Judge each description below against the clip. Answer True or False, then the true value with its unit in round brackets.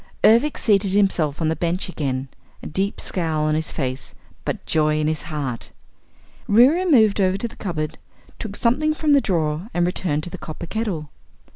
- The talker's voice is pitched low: False (175 Hz)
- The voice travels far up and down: True (5.8 semitones)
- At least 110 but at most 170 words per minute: False (180 wpm)